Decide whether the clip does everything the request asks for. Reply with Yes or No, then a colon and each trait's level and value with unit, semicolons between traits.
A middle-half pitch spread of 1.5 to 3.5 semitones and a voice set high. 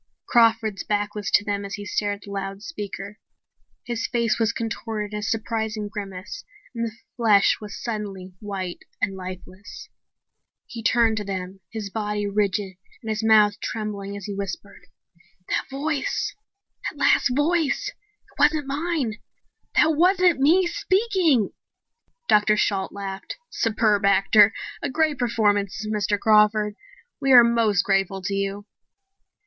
Yes: average, 2.8 semitones; high, 210 Hz